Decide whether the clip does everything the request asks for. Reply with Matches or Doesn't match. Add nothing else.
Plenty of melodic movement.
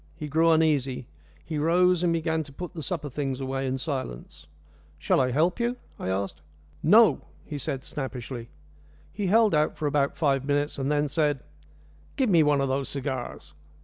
Doesn't match